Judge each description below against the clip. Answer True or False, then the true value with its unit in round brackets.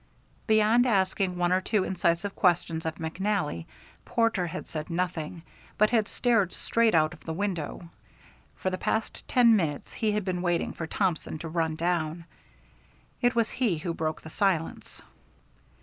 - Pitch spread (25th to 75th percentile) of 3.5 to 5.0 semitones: True (4.4 semitones)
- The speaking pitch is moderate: True (180 Hz)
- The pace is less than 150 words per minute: False (160 wpm)